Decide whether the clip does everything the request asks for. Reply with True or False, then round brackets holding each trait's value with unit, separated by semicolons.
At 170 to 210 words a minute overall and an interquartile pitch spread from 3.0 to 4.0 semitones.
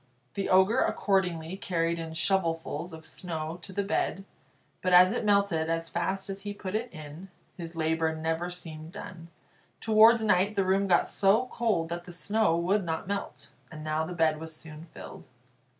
True (180 wpm; 3.4 semitones)